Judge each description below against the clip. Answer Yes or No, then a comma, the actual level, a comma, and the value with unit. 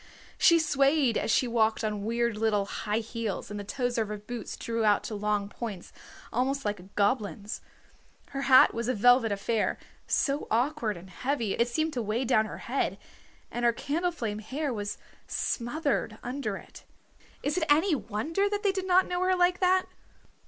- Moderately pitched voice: No, high, 235 Hz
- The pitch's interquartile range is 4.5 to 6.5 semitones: Yes, average, 5.3 semitones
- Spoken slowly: No, average, 180 wpm